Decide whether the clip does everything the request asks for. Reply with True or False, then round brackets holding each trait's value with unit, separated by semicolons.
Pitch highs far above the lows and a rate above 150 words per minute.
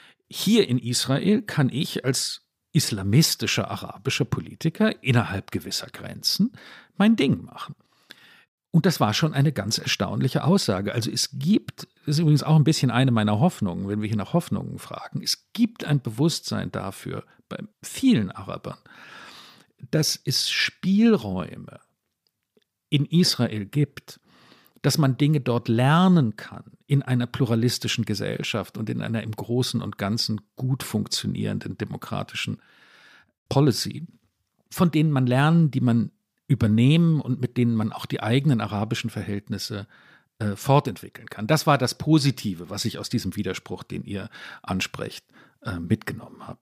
False (5.9 semitones; 140 wpm)